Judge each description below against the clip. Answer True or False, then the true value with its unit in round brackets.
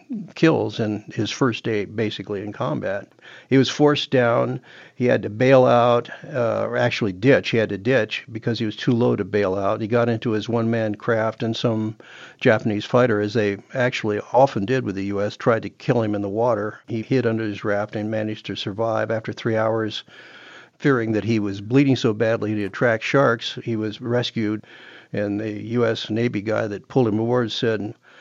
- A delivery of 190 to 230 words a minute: True (200 wpm)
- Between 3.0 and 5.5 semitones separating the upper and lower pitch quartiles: False (2.5 semitones)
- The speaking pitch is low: True (115 Hz)